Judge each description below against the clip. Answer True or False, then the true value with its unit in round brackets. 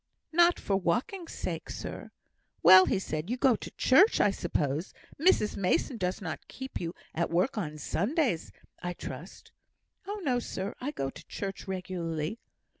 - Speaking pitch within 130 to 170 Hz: False (195 Hz)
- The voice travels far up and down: True (7.2 semitones)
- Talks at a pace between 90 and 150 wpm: False (160 wpm)